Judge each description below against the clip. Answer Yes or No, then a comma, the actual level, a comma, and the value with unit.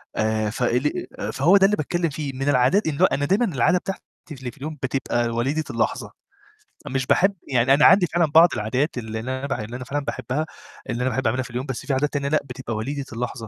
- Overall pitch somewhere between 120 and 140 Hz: Yes, low, 135 Hz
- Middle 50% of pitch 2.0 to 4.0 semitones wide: Yes, average, 3.6 semitones